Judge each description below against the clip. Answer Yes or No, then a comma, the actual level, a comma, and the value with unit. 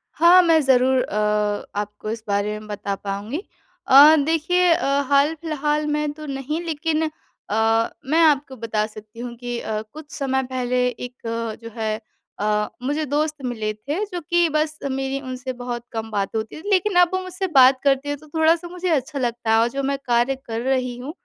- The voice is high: Yes, very high, 265 Hz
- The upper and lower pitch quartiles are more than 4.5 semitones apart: Yes, average, 5.0 semitones